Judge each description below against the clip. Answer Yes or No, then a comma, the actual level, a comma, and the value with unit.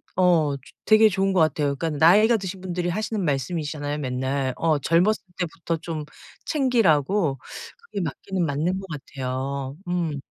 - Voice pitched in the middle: Yes, medium, 165 Hz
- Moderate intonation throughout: Yes, average, 4.7 semitones